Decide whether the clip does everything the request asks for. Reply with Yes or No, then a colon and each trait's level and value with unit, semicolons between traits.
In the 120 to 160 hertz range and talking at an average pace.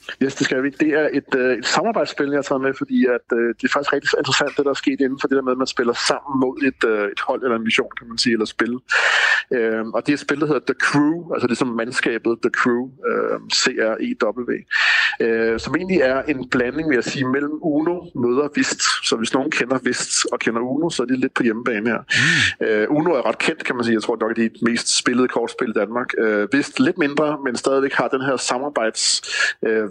No: low, 135 Hz; fast, 250 wpm